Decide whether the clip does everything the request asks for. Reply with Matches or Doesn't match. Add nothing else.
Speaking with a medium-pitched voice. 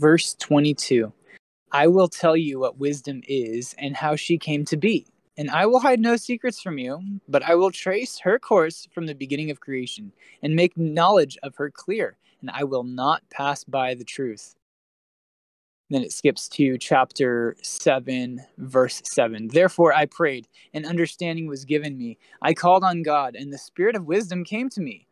Matches